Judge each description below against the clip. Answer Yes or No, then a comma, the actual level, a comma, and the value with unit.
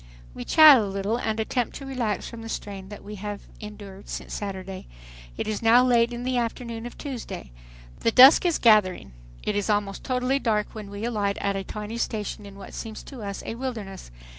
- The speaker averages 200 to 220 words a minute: Yes, fast, 205 wpm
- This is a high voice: Yes, high, 215 Hz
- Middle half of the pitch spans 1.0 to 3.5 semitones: Yes, average, 3.0 semitones